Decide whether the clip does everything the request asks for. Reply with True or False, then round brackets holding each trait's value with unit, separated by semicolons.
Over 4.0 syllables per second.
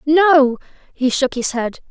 False (3.5 syllables/s)